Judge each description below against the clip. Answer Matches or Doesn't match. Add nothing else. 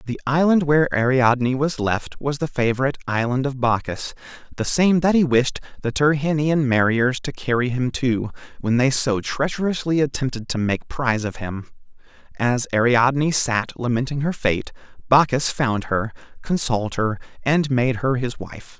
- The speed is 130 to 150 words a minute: Doesn't match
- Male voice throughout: Matches